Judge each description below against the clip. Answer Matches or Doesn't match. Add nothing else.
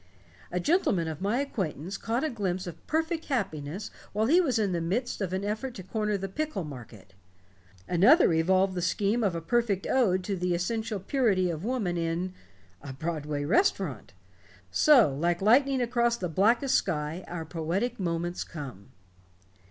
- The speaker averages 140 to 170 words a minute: Matches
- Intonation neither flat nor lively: Doesn't match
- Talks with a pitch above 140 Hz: Matches